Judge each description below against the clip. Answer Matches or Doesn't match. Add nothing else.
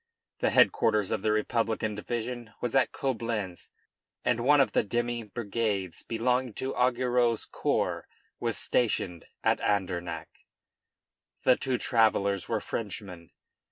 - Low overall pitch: Matches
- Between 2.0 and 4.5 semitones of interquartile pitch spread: Matches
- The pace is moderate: Doesn't match